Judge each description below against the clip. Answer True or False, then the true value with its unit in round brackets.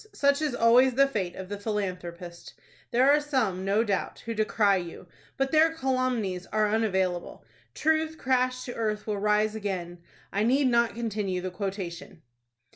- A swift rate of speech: False (160 wpm)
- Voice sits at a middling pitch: False (215 Hz)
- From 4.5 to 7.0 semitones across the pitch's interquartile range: True (5.2 semitones)